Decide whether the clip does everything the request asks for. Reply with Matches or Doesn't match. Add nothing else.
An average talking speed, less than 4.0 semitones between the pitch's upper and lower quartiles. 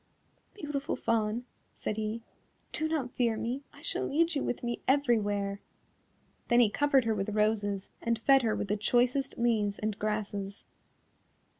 Matches